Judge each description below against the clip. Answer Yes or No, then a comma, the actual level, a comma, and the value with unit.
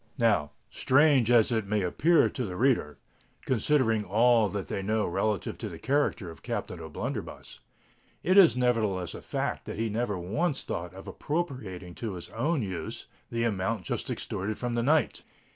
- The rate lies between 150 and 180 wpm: Yes, average, 160 wpm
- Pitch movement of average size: Yes, average, 5.0 semitones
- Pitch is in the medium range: No, low, 110 Hz